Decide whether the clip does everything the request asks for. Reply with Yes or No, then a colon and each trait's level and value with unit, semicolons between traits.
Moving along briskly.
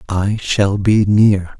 No: average, 150 wpm